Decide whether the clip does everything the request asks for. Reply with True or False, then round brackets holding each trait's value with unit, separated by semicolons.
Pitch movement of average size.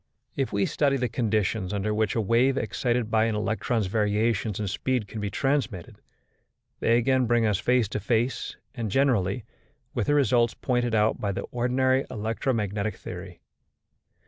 True (3.1 semitones)